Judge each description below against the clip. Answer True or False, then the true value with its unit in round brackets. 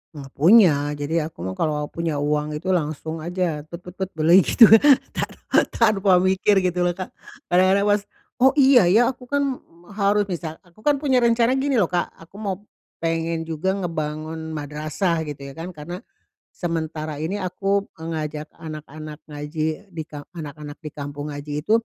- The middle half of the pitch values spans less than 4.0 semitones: False (4.3 semitones)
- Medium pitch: True (165 Hz)